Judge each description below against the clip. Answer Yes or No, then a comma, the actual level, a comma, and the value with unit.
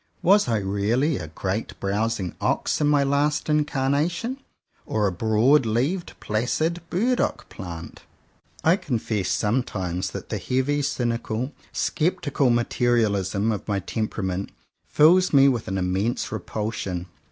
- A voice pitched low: Yes, low, 115 Hz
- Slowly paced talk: Yes, slow, 130 wpm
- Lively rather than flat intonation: Yes, wide, 6.5 semitones